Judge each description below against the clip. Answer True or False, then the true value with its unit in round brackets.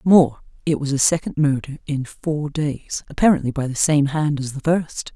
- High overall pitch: False (145 Hz)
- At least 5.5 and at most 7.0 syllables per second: False (4.7 syllables/s)